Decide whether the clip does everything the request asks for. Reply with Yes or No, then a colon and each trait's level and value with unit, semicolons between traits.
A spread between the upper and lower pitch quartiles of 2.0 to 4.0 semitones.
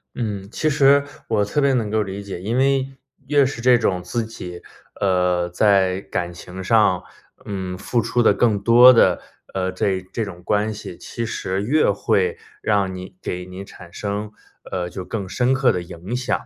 No: average, 4.6 semitones